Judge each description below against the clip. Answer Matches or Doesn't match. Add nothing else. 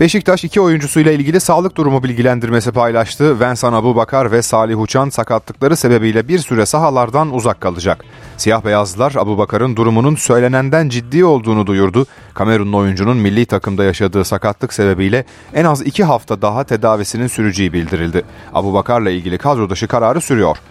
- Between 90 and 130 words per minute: Doesn't match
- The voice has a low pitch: Matches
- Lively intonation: Doesn't match